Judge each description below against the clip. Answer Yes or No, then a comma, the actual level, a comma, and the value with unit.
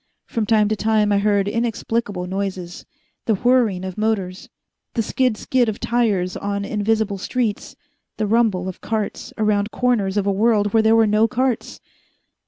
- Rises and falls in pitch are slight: Yes, narrow, 2.2 semitones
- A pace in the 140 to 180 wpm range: Yes, average, 165 wpm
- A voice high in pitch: Yes, high, 215 Hz